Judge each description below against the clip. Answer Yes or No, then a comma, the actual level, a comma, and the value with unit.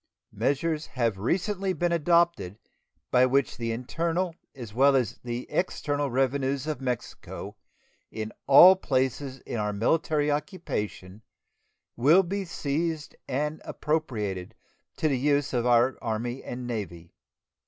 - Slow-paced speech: Yes, slow, 125 wpm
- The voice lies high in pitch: No, low, 135 Hz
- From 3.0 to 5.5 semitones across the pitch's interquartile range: Yes, average, 4.9 semitones